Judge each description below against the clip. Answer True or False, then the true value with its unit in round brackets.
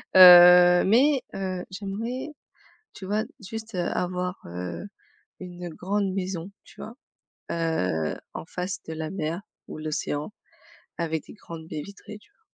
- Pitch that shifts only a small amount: False (3.6 semitones)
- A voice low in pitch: False (180 Hz)